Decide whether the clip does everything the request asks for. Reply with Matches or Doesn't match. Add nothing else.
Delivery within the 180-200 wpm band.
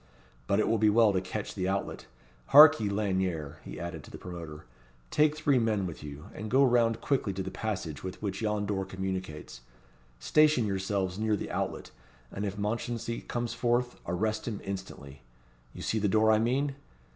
Matches